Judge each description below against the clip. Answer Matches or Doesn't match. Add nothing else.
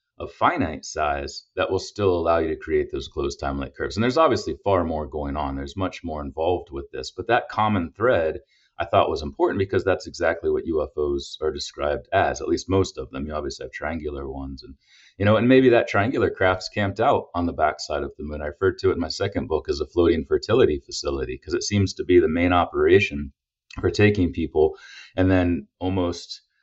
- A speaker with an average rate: Doesn't match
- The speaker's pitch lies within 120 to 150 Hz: Doesn't match